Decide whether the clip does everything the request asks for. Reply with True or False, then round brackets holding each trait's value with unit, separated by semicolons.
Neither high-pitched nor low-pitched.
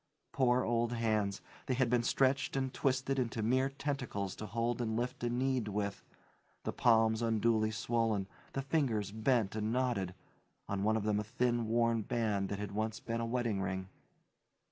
False (115 Hz)